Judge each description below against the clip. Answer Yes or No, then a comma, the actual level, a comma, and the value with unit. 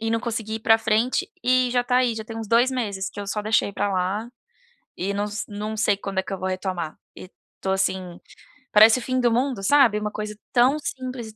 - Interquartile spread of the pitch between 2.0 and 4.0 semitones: Yes, average, 3.2 semitones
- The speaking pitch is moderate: No, high, 215 Hz